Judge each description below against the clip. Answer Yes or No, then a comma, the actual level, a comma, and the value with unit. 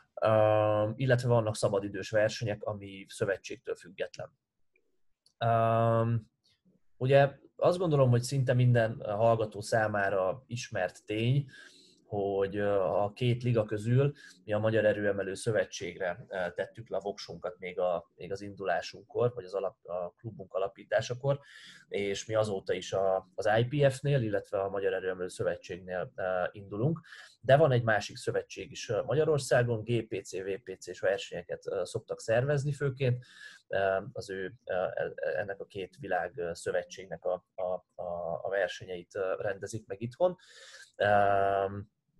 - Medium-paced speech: Yes, average, 130 wpm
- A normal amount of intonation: No, wide, 6.3 semitones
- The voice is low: Yes, low, 115 Hz